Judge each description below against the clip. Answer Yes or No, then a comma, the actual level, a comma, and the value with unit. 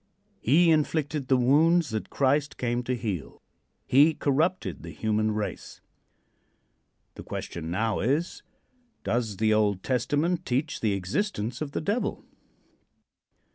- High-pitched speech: No, low, 130 Hz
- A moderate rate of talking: No, slow, 125 wpm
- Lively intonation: Yes, wide, 6.1 semitones